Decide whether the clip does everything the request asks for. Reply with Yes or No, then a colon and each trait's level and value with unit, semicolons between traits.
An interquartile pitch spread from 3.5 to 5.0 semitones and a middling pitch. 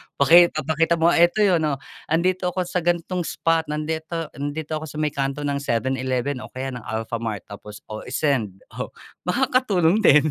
Yes: average, 4.6 semitones; medium, 155 Hz